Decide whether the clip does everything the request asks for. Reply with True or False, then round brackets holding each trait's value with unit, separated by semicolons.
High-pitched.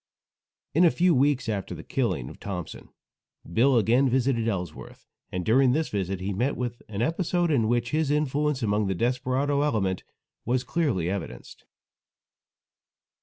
False (125 Hz)